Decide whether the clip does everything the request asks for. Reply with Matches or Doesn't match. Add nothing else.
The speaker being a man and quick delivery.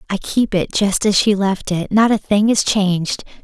Doesn't match